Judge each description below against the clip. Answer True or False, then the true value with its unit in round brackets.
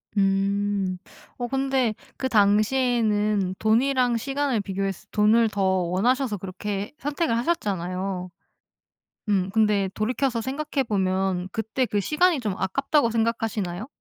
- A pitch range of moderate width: True (4.5 semitones)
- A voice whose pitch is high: True (215 Hz)